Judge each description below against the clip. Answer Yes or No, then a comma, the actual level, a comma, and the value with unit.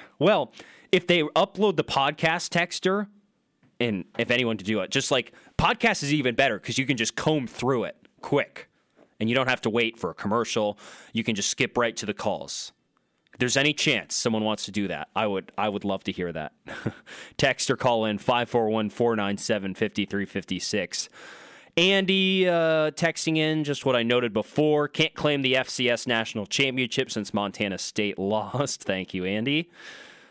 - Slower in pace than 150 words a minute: No, average, 175 wpm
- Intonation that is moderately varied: No, wide, 6.3 semitones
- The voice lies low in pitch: Yes, low, 125 Hz